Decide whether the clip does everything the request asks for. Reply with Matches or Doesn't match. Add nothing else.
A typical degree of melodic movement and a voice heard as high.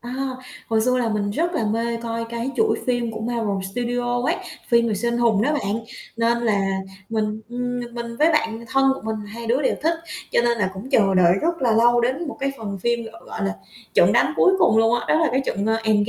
Doesn't match